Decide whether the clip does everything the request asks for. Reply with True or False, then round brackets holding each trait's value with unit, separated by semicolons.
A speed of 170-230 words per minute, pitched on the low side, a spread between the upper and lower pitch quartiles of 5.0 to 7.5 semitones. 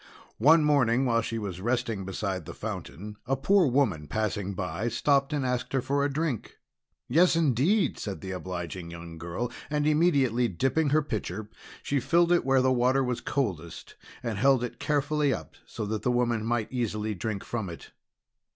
True (180 wpm; 120 Hz; 5.5 semitones)